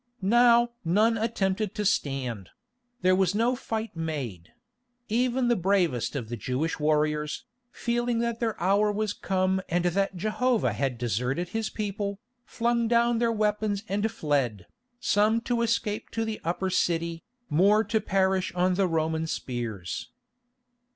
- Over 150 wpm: No, average, 145 wpm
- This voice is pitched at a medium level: No, high, 195 Hz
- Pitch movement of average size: No, wide, 5.8 semitones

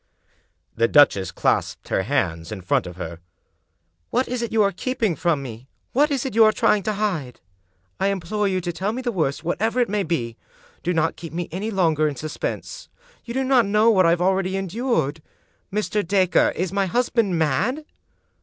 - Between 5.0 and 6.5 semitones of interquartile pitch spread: Yes, wide, 5.6 semitones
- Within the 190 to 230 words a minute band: Yes, average, 200 wpm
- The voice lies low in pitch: No, high, 190 Hz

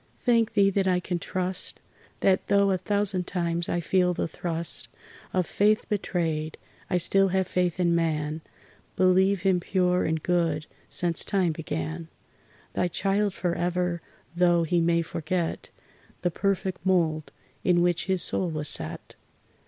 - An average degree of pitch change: No, narrow, 2.1 semitones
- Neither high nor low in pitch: Yes, medium, 180 Hz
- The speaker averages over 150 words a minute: No, average, 145 wpm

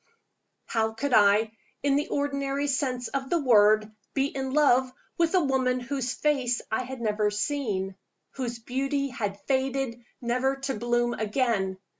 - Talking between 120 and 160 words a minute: Yes, average, 150 wpm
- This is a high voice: Yes, very high, 255 Hz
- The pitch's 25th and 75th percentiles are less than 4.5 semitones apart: Yes, average, 3.5 semitones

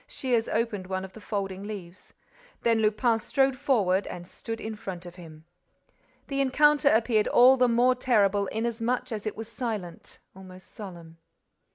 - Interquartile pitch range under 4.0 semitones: No, average, 4.3 semitones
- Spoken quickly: No, average, 160 wpm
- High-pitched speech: Yes, high, 220 Hz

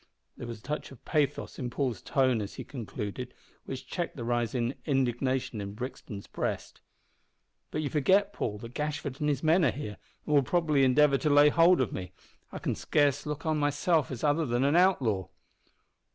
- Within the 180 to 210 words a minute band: Yes, average, 190 wpm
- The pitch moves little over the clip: No, average, 3.8 semitones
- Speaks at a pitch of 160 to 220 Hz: No, low, 135 Hz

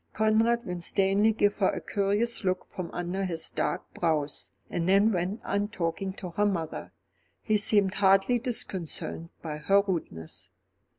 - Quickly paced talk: No, average, 145 wpm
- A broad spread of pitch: No, average, 3.1 semitones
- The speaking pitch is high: Yes, high, 195 Hz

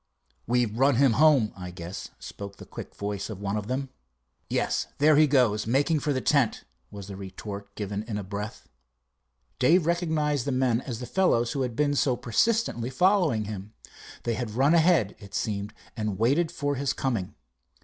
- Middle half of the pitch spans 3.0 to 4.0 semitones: No, wide, 5.6 semitones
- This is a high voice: No, low, 120 Hz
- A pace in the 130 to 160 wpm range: No, average, 180 wpm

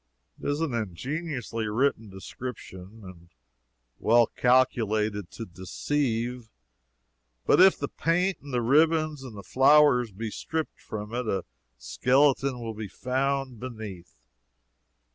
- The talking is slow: Yes, slow, 125 wpm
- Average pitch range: Yes, average, 4.6 semitones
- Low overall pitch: Yes, low, 120 Hz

